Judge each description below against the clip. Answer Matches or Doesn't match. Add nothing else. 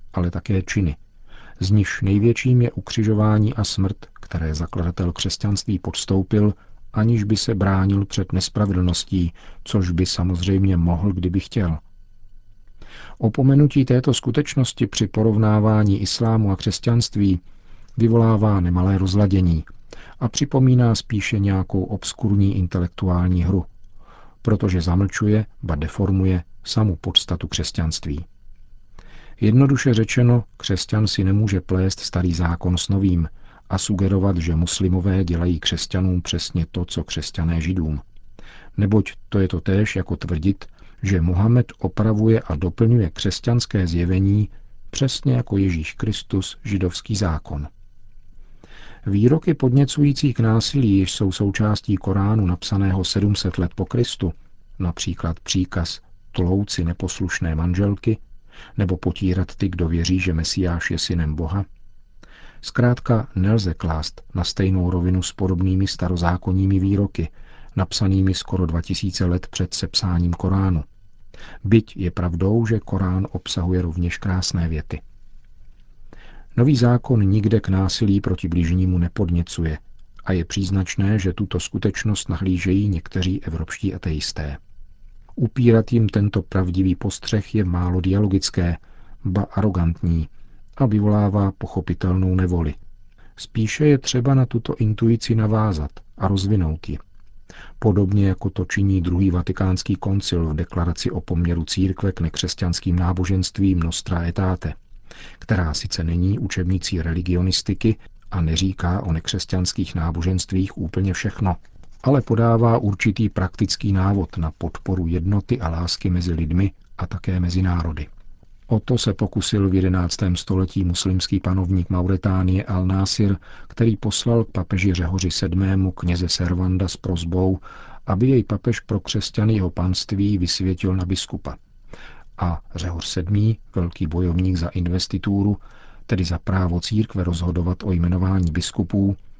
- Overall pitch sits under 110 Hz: Matches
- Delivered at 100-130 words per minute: Matches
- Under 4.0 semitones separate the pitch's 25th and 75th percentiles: Matches